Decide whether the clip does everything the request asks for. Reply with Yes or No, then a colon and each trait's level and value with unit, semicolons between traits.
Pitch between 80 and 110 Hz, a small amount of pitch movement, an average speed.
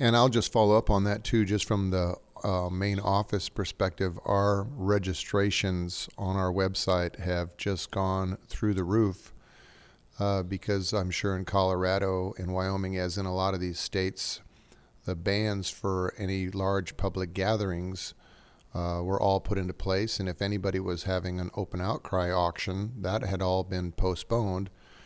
Yes: very low, 95 Hz; narrow, 1.6 semitones; average, 165 wpm